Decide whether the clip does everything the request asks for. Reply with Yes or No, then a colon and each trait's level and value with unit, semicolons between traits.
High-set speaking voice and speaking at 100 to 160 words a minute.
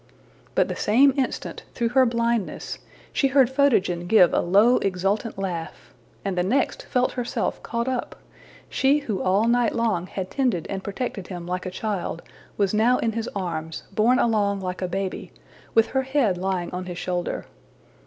No: high, 210 Hz; average, 175 wpm